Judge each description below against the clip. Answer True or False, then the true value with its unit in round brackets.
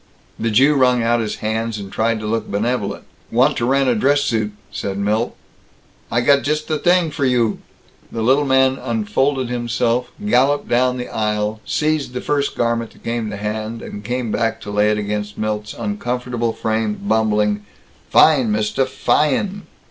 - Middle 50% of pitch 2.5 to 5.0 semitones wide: True (3.7 semitones)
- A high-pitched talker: False (120 Hz)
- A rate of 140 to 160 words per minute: False (175 wpm)